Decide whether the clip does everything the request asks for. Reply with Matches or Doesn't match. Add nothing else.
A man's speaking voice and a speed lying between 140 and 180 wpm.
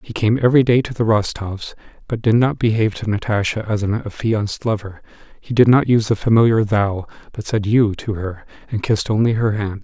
Doesn't match